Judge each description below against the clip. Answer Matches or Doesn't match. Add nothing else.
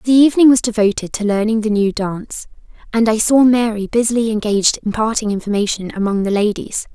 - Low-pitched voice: Doesn't match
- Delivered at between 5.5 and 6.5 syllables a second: Matches